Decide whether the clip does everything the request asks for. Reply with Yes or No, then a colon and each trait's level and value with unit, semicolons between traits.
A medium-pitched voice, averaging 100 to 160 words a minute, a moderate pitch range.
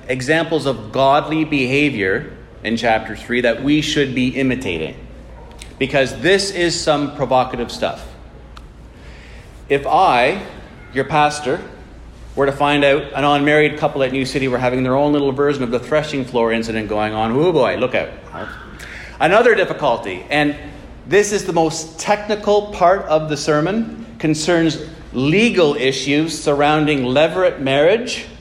Yes: medium, 145 Hz; average, 140 wpm; average, 3.6 semitones